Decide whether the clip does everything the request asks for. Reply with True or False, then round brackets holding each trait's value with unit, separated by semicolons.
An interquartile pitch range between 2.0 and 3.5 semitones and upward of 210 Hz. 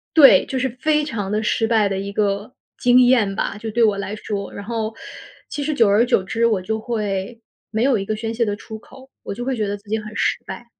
True (2.9 semitones; 220 Hz)